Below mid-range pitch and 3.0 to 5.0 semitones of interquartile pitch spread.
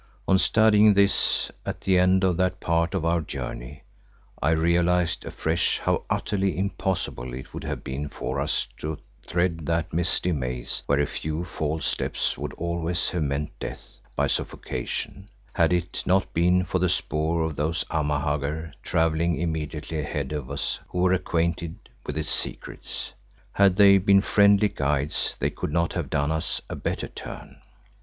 Yes: very low, 85 Hz; average, 3.3 semitones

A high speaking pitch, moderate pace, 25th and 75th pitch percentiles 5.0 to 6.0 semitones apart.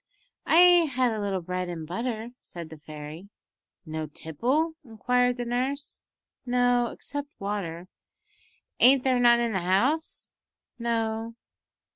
No: high, 230 Hz; slow, 125 wpm; wide, 5.6 semitones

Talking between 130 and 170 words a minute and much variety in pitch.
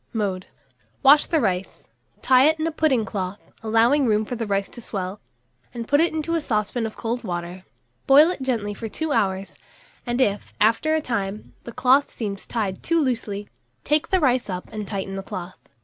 No: average, 195 wpm; wide, 5.7 semitones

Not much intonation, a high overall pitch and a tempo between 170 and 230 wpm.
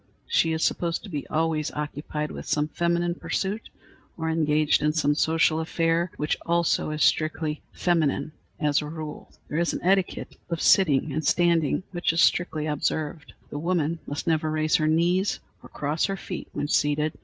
No: narrow, 2.1 semitones; medium, 160 Hz; average, 175 wpm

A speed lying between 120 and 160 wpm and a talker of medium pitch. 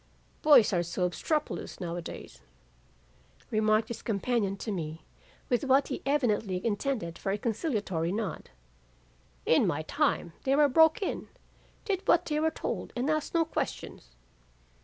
No: average, 150 wpm; high, 225 Hz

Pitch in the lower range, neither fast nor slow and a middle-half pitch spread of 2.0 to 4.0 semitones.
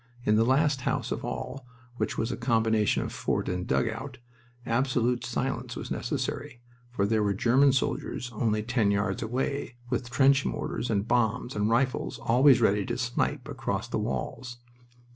Yes: low, 120 Hz; average, 160 wpm; average, 2.9 semitones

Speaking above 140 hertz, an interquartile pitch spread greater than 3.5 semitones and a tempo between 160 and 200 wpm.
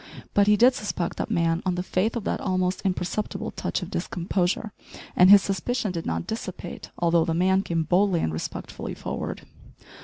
No: medium, 185 Hz; average, 3.0 semitones; average, 180 wpm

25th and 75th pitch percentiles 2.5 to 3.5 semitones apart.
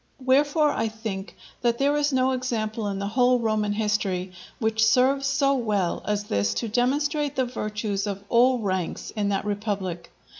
No: average, 4.1 semitones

